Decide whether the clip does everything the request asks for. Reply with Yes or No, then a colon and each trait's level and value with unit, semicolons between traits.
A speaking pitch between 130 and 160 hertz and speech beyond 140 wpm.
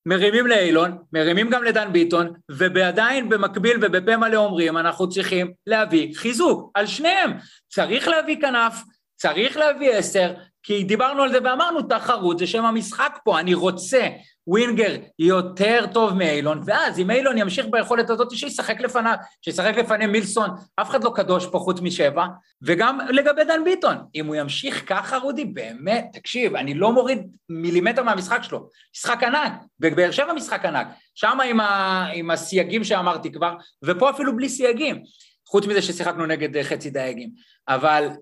No: high, 205 Hz; fast, 150 wpm